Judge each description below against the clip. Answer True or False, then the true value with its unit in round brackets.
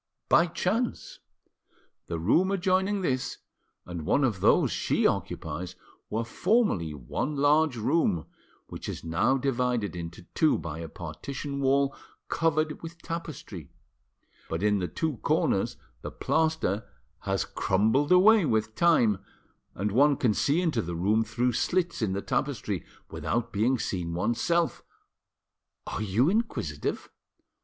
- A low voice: True (125 Hz)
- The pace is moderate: False (130 wpm)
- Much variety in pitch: True (8.8 semitones)